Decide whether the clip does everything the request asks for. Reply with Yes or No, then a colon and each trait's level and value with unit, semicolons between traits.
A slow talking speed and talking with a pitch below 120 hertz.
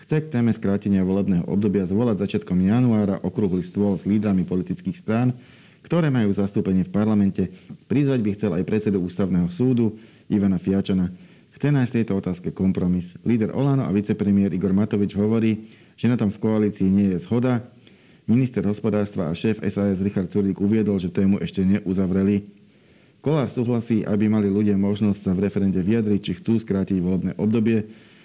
No: average, 160 wpm; low, 100 Hz